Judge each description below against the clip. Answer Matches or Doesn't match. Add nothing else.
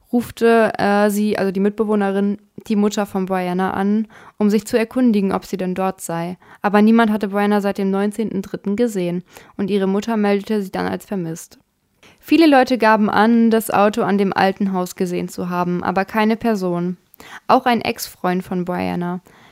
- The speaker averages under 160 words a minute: Doesn't match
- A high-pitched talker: Matches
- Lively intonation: Doesn't match